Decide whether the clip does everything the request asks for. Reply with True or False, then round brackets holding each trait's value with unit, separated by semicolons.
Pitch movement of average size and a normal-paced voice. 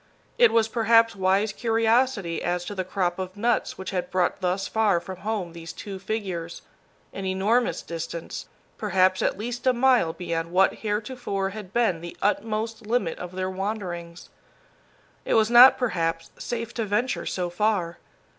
True (4.0 semitones; 160 wpm)